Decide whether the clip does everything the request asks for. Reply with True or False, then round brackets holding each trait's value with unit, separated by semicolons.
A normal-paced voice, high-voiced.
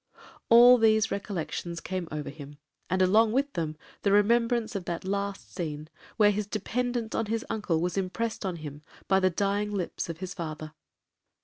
True (175 wpm; 195 Hz)